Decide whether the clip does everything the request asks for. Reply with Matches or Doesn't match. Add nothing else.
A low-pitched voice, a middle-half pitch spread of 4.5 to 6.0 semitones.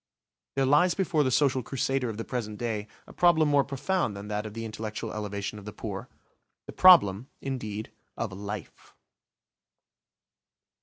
Matches